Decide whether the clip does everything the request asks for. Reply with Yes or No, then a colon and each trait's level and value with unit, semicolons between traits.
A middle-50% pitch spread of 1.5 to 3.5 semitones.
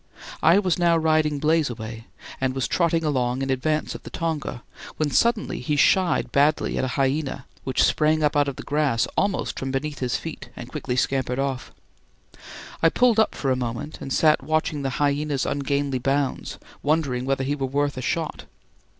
Yes: average, 2.9 semitones